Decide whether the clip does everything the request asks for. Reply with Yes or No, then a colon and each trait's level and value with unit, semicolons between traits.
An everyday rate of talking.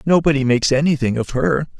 Yes: average, 165 wpm